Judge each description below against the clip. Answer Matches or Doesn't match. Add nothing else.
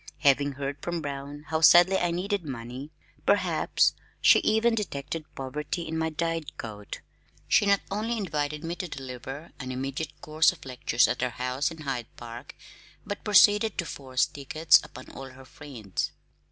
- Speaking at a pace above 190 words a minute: Doesn't match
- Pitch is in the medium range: Matches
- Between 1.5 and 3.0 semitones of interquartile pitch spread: Doesn't match